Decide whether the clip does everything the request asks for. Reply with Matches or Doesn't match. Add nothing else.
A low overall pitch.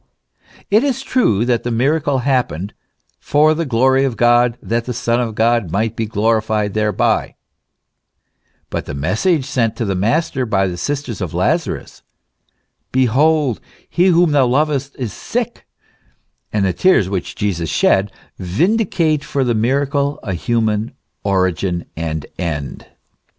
Matches